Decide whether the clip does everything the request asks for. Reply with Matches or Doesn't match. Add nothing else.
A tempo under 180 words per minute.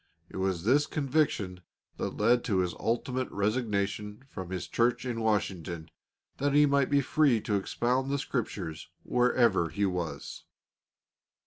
Matches